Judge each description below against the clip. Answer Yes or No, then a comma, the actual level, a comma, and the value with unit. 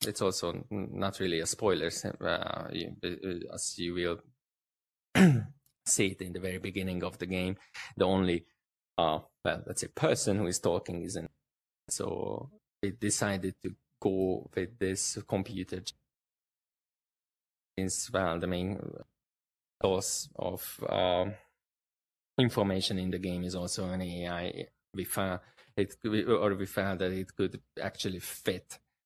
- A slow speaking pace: Yes, slow, 130 wpm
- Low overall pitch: Yes, very low, 95 Hz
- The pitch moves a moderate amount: No, narrow, 1.7 semitones